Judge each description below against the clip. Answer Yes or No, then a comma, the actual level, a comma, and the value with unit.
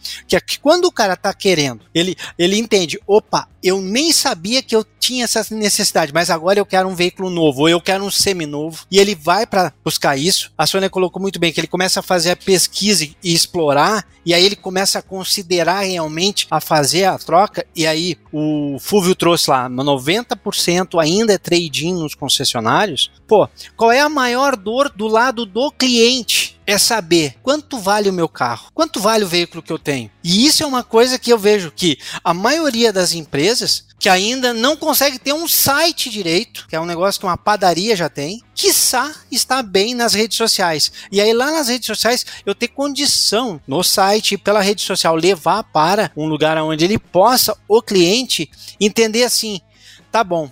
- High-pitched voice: Yes, high, 195 Hz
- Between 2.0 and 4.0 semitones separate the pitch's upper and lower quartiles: No, average, 5.3 semitones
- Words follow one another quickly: Yes, fast, 195 wpm